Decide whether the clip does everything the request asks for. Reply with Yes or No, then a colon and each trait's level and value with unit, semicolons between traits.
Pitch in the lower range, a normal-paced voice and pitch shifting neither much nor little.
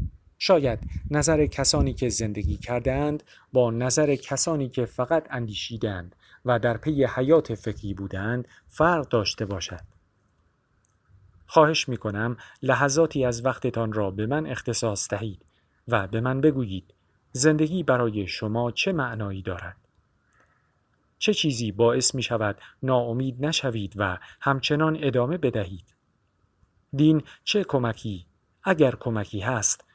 Yes: low, 120 Hz; average, 120 wpm; average, 4.9 semitones